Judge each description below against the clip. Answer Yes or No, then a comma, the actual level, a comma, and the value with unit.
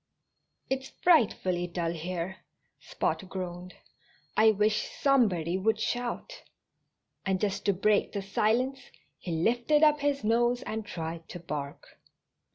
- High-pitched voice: Yes, high, 205 Hz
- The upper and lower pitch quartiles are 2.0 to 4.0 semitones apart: No, average, 5.3 semitones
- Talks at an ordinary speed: No, slow, 125 wpm